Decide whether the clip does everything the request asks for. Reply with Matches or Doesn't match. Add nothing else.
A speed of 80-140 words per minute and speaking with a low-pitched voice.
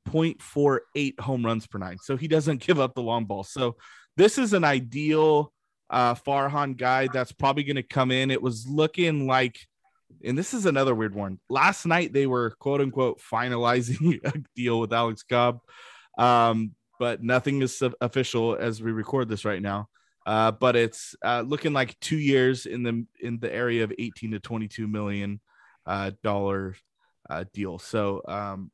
Doesn't match